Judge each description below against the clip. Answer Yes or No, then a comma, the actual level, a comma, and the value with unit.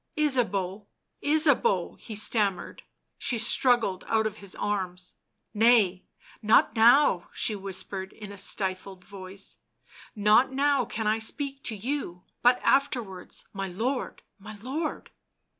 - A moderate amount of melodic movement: Yes, average, 4.5 semitones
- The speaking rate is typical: No, slow, 125 wpm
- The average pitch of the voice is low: No, high, 215 Hz